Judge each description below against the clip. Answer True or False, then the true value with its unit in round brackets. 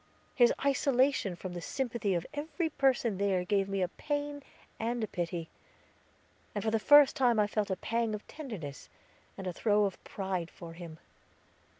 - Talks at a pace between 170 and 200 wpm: True (175 wpm)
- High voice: True (210 Hz)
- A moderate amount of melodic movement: False (5.8 semitones)